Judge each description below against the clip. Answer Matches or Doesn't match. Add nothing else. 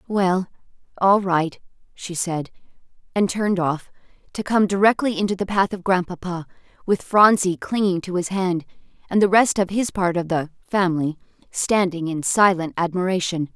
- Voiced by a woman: Matches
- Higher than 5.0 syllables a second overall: Doesn't match